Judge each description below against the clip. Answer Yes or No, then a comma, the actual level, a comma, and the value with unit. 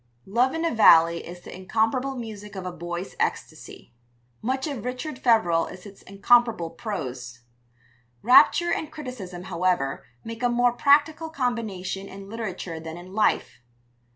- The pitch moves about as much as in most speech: No, wide, 5.7 semitones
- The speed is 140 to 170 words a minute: Yes, average, 145 wpm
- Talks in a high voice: Yes, high, 210 Hz